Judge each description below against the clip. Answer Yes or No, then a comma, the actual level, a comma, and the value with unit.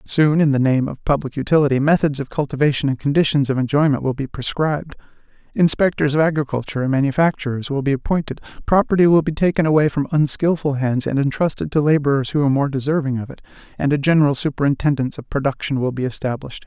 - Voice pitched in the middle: Yes, medium, 145 Hz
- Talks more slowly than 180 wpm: No, average, 185 wpm